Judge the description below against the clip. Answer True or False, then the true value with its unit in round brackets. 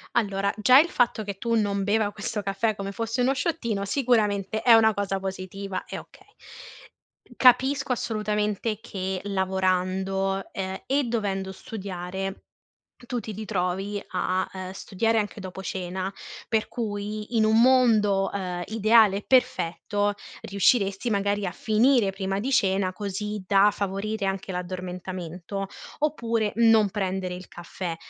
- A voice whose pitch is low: False (200 Hz)